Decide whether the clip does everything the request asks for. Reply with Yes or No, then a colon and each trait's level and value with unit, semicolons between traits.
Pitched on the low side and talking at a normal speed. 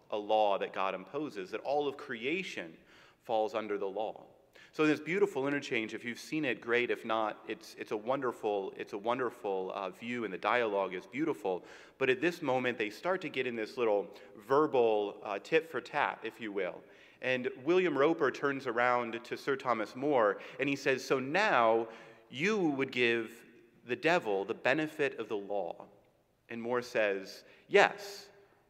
Yes: low, 120 Hz; average, 180 wpm